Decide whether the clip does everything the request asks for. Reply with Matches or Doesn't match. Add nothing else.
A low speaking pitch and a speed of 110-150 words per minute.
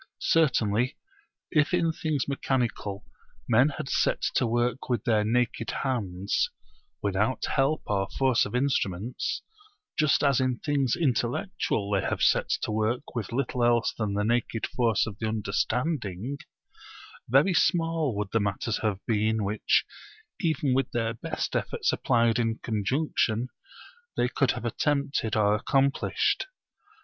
Matches